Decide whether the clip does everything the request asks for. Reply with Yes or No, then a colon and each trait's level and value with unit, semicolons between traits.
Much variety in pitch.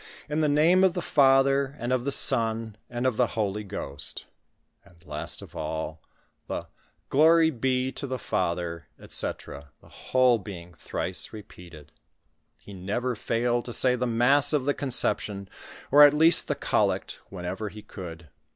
Yes: wide, 6.8 semitones